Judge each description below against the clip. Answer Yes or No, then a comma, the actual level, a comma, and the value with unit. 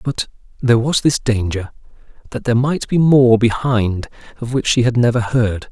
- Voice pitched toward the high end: No, low, 120 Hz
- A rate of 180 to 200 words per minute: No, average, 170 wpm